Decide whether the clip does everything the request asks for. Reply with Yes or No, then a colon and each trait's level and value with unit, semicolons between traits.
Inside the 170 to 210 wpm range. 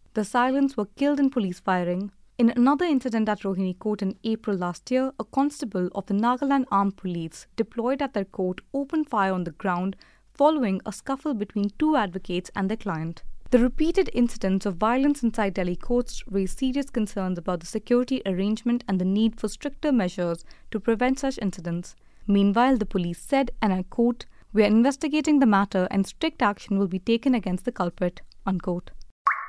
Yes: average, 180 wpm